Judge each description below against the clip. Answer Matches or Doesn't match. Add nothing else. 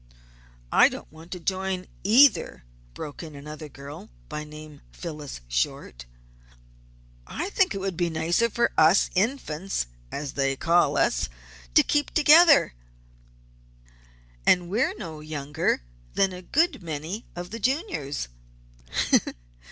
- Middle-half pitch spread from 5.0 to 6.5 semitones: Matches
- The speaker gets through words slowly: Matches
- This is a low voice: Doesn't match